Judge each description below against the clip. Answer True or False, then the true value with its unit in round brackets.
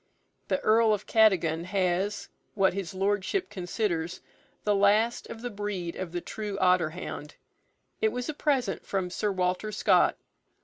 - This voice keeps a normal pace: True (150 wpm)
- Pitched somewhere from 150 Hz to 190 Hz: False (200 Hz)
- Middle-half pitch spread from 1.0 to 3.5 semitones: True (3.0 semitones)